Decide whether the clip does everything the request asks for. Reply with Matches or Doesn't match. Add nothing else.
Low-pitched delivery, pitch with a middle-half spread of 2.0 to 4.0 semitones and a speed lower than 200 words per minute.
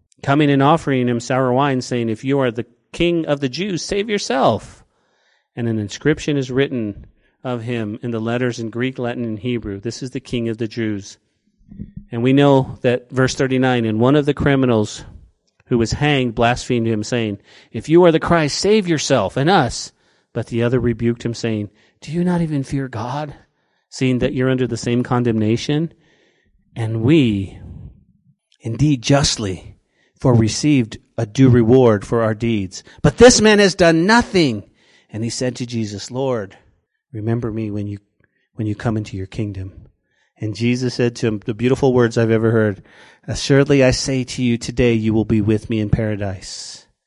Matches